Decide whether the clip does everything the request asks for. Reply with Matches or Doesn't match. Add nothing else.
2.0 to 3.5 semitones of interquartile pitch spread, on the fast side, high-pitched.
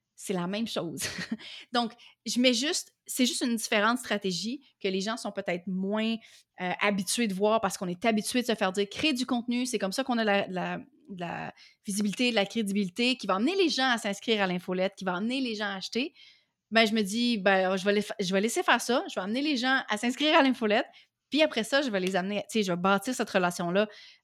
Doesn't match